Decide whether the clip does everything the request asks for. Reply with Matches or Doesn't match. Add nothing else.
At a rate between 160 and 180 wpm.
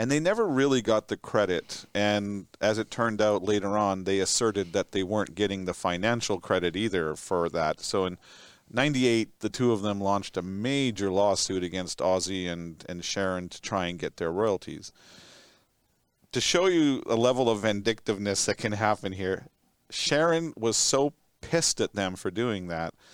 Matches